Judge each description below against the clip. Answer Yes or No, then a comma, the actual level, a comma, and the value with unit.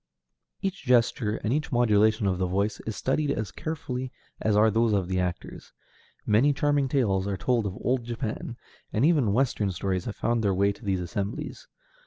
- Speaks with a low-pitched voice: Yes, low, 110 Hz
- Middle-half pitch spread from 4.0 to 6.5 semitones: Yes, average, 4.4 semitones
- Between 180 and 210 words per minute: Yes, average, 185 wpm